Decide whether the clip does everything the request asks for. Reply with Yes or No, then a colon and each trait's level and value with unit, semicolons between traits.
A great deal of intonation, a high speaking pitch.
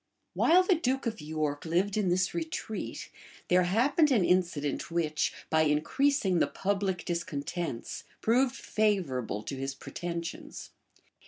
No: wide, 6.4 semitones; medium, 180 Hz